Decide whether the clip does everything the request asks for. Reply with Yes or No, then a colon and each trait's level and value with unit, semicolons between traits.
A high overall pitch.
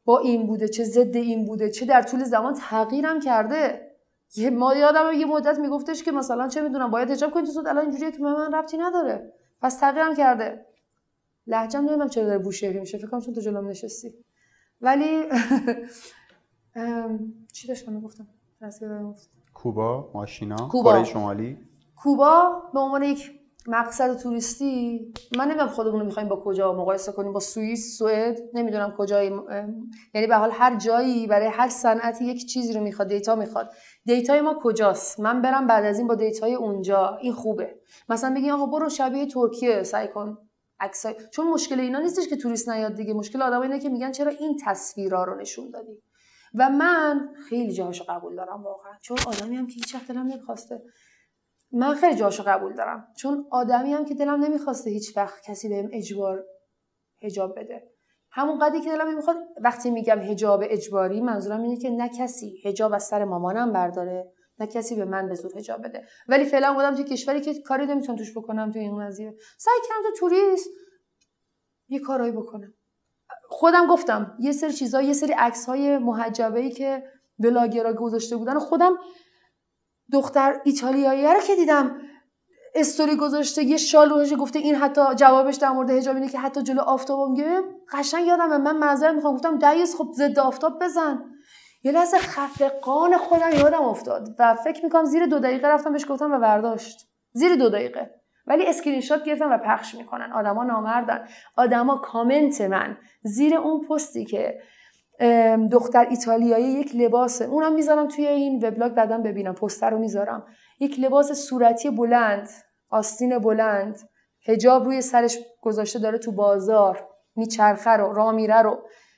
Yes: high, 245 Hz